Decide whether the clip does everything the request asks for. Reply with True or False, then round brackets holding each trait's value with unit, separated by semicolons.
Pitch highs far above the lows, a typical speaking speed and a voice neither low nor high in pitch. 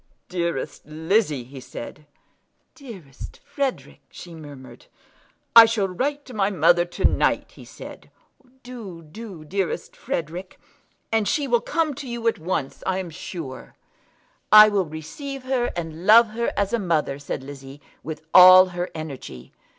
True (6.6 semitones; 150 wpm; 180 Hz)